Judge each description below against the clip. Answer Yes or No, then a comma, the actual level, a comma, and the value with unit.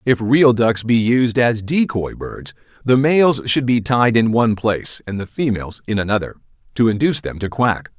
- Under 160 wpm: No, average, 195 wpm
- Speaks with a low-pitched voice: Yes, low, 120 Hz